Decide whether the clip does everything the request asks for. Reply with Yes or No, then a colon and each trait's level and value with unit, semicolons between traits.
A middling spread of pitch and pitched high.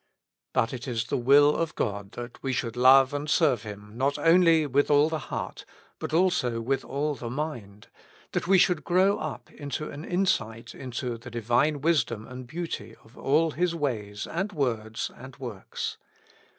No: average, 5.0 semitones; low, 135 Hz